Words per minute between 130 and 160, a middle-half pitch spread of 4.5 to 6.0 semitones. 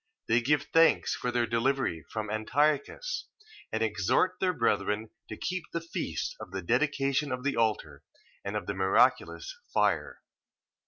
Yes: average, 150 wpm; wide, 5.5 semitones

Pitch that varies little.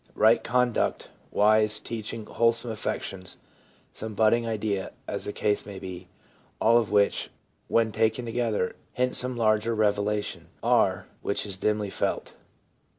Yes: narrow, 2.1 semitones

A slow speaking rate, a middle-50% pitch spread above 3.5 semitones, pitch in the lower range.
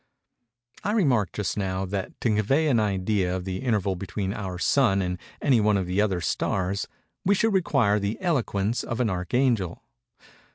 No: average, 170 wpm; average, 4.6 semitones; low, 105 Hz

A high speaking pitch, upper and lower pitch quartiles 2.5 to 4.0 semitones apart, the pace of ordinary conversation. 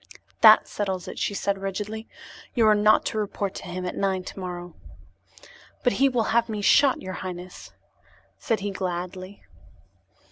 Yes: high, 200 Hz; average, 2.8 semitones; average, 155 wpm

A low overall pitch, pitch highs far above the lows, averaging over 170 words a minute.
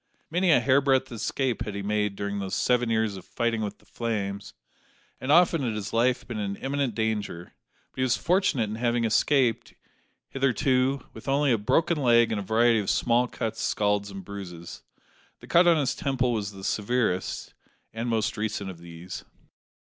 No: low, 115 Hz; average, 4.2 semitones; average, 180 wpm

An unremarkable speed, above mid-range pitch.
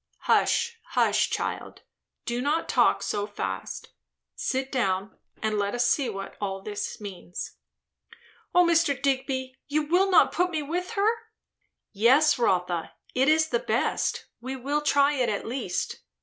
Yes: average, 150 wpm; very high, 265 Hz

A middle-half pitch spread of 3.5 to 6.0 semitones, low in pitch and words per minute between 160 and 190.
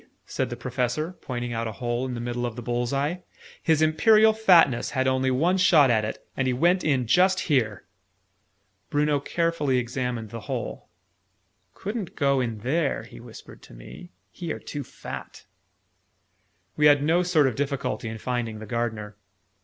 Yes: average, 4.7 semitones; low, 130 Hz; average, 170 wpm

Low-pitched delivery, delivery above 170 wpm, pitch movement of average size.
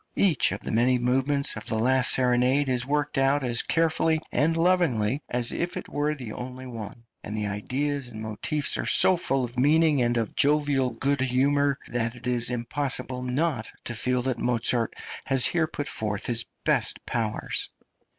Yes: low, 130 Hz; average, 180 wpm; average, 3.3 semitones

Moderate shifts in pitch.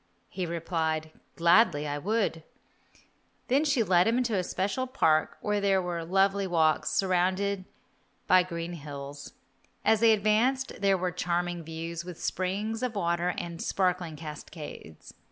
Yes: average, 3.4 semitones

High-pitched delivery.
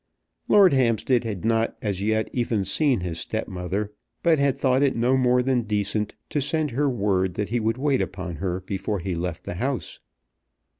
No: low, 110 Hz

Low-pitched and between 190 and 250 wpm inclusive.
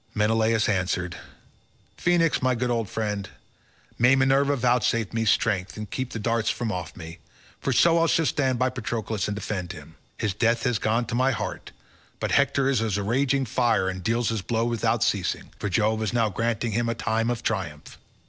Yes: low, 115 Hz; average, 195 wpm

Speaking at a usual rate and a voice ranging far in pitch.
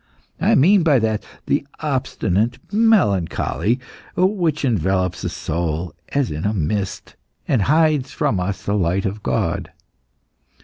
No: slow, 130 wpm; wide, 7.7 semitones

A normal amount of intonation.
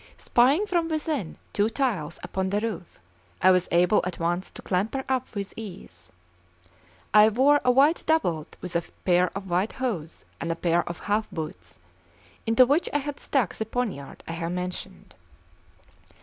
No: wide, 6.8 semitones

